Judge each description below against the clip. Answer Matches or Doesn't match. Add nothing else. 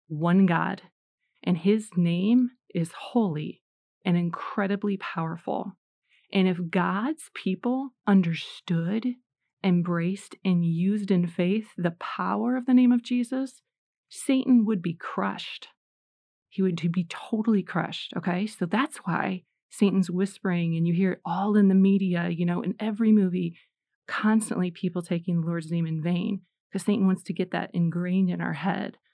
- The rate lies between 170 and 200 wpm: Doesn't match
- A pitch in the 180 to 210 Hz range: Matches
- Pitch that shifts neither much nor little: Matches